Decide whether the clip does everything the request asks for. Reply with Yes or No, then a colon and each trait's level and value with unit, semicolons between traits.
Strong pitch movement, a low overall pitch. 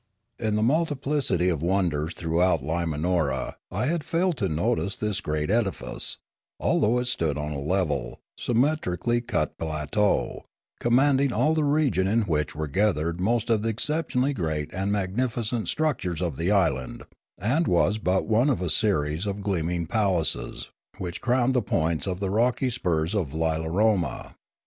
Yes: wide, 6.5 semitones; very low, 95 Hz